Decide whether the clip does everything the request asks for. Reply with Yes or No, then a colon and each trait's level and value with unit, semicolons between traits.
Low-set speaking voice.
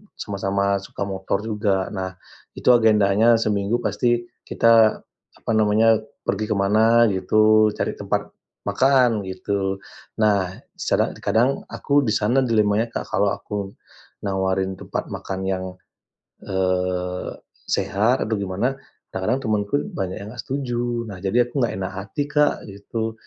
Yes: low, 105 Hz